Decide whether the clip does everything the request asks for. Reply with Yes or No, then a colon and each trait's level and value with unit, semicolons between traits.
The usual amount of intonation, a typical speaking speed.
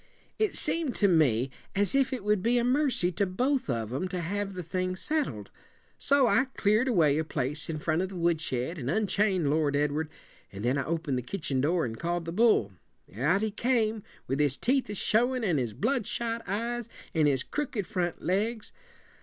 No: wide, 7.4 semitones; average, 195 wpm